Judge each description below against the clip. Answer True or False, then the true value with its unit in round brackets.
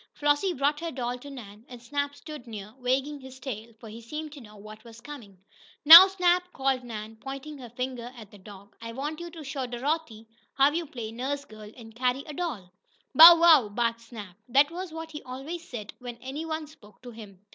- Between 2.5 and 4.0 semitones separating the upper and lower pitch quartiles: False (4.8 semitones)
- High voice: True (260 Hz)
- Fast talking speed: True (210 wpm)